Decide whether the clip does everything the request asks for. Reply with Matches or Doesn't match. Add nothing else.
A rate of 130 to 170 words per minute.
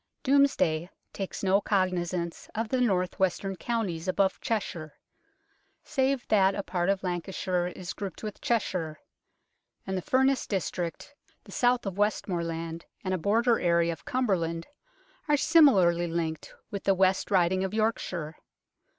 Matches